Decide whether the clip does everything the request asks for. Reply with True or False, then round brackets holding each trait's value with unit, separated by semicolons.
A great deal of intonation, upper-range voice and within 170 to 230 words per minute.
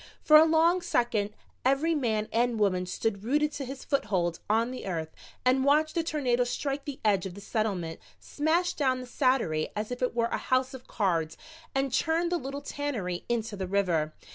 True (6.1 semitones; 245 Hz; 190 wpm)